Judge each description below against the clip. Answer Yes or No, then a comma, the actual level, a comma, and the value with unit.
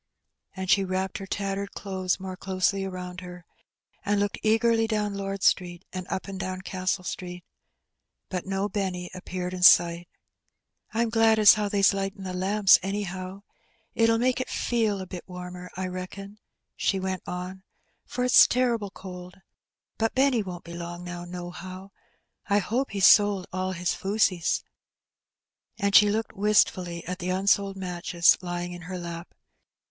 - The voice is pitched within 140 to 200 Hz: Yes, high, 190 Hz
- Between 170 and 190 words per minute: No, average, 160 wpm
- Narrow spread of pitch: Yes, narrow, 2.1 semitones